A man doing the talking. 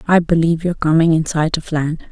No: female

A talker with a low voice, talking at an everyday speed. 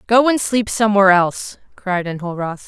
No: high, 200 Hz; average, 155 wpm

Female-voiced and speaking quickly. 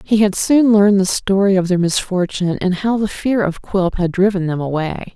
Yes: female; fast, 220 wpm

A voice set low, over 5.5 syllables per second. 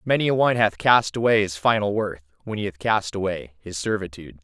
Yes: low, 100 Hz; 5.9 syllables/s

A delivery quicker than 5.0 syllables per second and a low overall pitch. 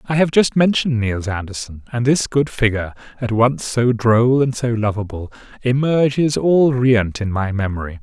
No: 4.9 syllables/s; low, 120 Hz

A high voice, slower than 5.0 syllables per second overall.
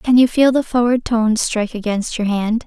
No: high, 230 Hz; 5.3 syllables/s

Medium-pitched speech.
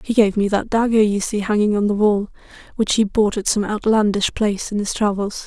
No: high, 210 Hz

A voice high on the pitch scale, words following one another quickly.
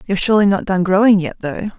Yes: high, 195 Hz; fast, 235 wpm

